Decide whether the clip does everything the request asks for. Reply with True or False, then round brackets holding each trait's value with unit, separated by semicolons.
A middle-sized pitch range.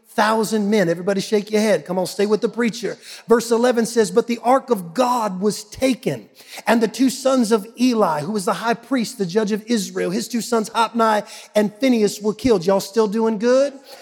False (2.2 semitones)